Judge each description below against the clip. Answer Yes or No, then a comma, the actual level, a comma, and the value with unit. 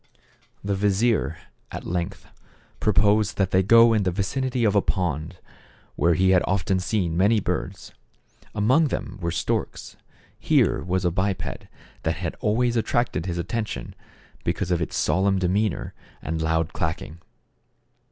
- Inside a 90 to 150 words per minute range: Yes, average, 145 wpm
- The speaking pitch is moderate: No, very low, 95 Hz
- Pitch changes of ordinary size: Yes, average, 3.7 semitones